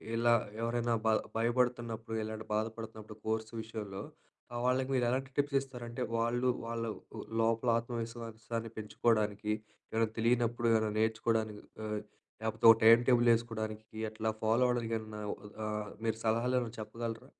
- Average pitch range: No, narrow, 1.3 semitones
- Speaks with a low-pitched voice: Yes, low, 115 Hz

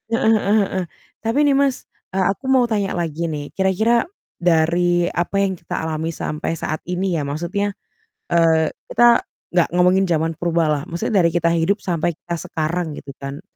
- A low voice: No, medium, 175 Hz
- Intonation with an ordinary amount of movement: Yes, average, 3.3 semitones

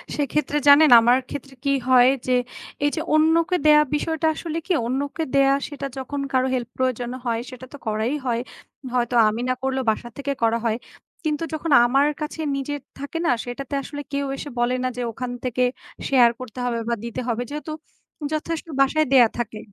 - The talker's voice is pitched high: Yes, very high, 265 Hz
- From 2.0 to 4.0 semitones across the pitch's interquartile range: Yes, average, 3.4 semitones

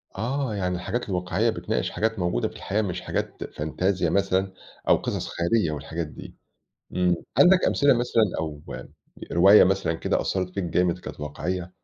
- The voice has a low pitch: Yes, very low, 90 Hz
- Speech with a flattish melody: No, average, 3.5 semitones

